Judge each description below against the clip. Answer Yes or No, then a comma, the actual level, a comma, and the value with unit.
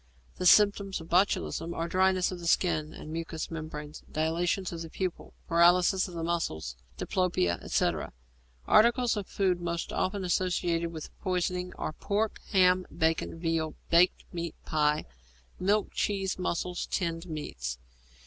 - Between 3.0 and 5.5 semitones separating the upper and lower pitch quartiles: No, narrow, 2.4 semitones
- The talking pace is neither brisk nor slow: No, slow, 130 wpm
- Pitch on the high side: No, medium, 175 Hz